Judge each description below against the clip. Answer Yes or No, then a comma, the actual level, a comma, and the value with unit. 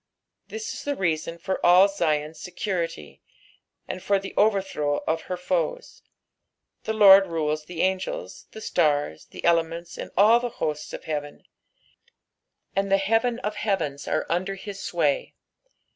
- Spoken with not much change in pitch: No, average, 3.9 semitones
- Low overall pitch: No, medium, 180 Hz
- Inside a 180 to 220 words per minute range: No, average, 145 wpm